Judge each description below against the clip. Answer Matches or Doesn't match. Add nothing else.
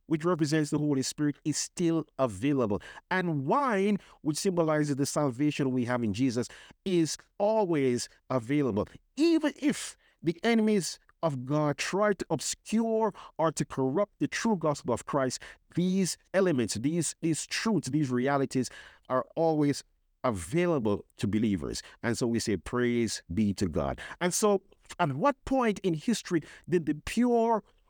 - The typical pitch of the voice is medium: Matches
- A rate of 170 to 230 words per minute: Doesn't match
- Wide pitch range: Matches